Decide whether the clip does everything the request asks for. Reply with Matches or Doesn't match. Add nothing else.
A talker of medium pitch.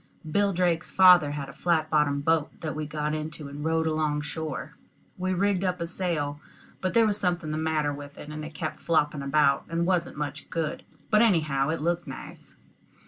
Matches